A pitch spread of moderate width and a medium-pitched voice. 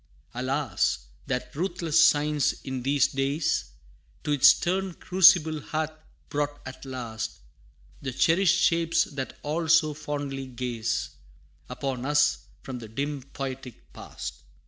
Yes: average, 3.4 semitones; medium, 145 Hz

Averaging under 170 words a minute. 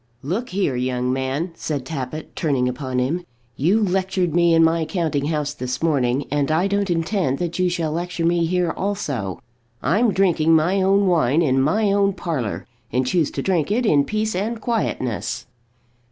No: average, 175 wpm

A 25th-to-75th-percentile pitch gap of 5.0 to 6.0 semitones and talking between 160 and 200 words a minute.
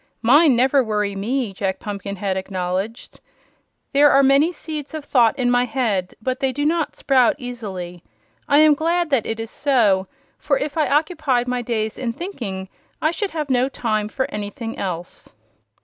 Yes: wide, 5.6 semitones; average, 170 wpm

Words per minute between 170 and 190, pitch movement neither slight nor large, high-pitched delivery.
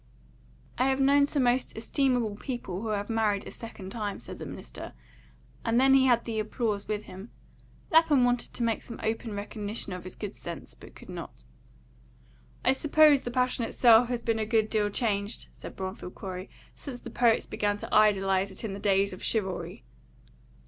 Yes: average, 185 wpm; average, 3.5 semitones; high, 220 Hz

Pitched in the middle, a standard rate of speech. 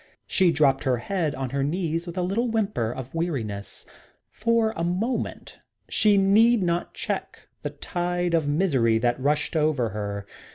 Yes: medium, 165 Hz; average, 160 wpm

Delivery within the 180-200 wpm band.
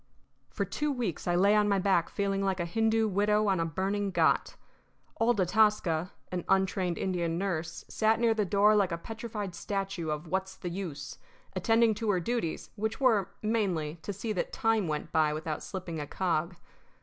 Yes: average, 185 wpm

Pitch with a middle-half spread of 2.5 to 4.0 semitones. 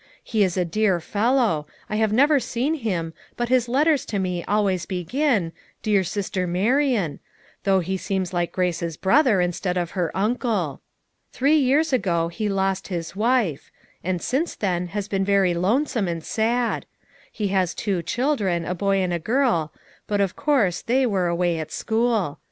No: average, 5.1 semitones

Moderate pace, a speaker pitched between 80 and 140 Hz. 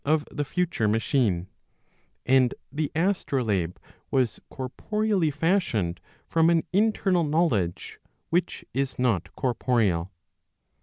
No: slow, 105 wpm; low, 135 Hz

